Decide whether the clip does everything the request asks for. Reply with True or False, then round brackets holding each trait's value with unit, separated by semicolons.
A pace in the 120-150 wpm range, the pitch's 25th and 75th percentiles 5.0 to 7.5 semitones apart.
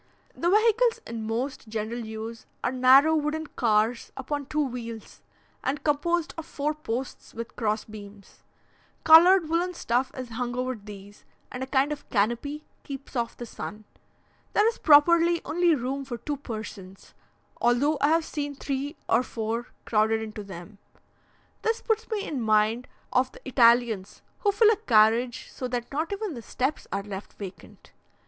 False (160 wpm; 5.3 semitones)